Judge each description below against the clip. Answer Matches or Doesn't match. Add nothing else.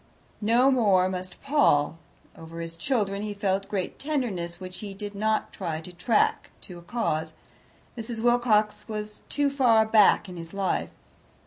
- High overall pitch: Matches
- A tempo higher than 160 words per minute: Doesn't match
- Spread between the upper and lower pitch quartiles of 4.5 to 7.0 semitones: Doesn't match